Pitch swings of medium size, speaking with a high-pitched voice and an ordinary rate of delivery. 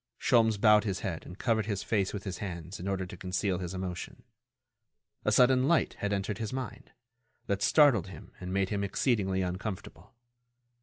No: average, 3.0 semitones; low, 100 Hz; average, 175 wpm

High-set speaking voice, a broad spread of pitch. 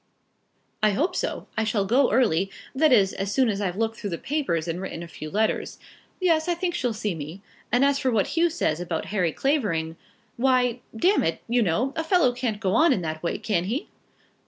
Yes: high, 220 Hz; wide, 6.5 semitones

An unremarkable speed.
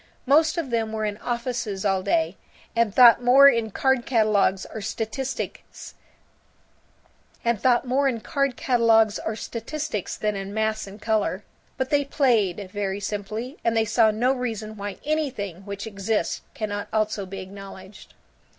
No: slow, 125 wpm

